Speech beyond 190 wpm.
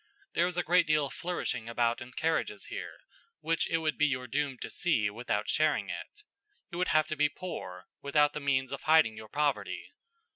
Yes: fast, 205 wpm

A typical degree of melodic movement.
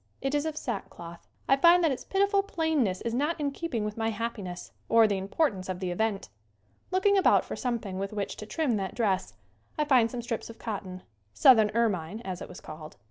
No: wide, 7.0 semitones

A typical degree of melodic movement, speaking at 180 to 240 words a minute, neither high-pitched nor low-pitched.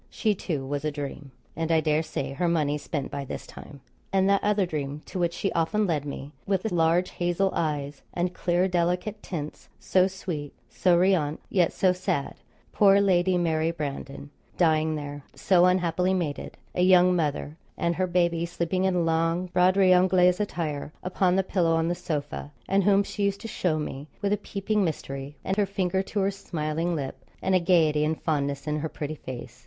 Yes: average, 3.5 semitones; average, 190 wpm; medium, 170 Hz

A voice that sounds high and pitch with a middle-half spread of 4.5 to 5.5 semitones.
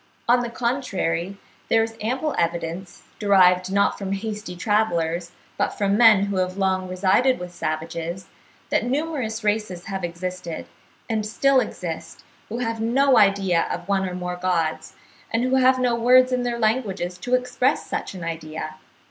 Yes: high, 200 Hz; average, 4.8 semitones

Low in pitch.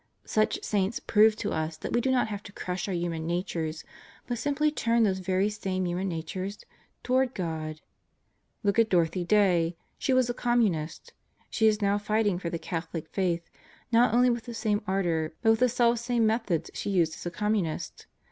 No: high, 200 Hz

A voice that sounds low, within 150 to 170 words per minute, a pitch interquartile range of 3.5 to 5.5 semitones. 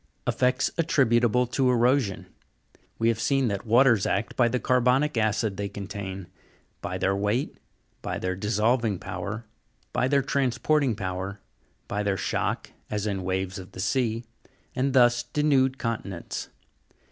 No: low, 115 Hz; average, 140 wpm; average, 4.3 semitones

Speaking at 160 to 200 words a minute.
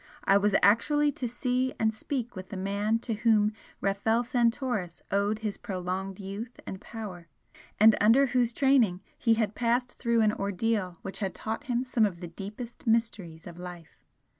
Yes: average, 170 wpm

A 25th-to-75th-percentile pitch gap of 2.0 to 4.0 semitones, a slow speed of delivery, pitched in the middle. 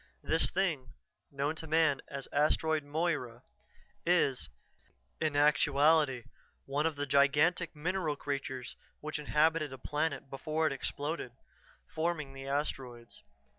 Yes: narrow, 2.6 semitones; slow, 120 wpm; medium, 150 Hz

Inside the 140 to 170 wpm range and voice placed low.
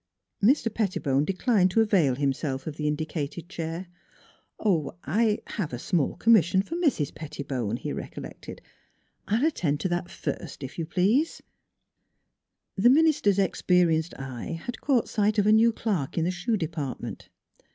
No: average, 160 wpm; medium, 180 Hz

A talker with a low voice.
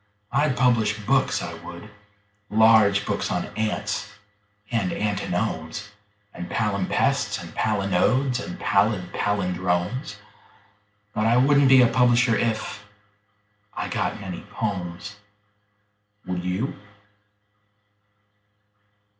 Yes: low, 105 Hz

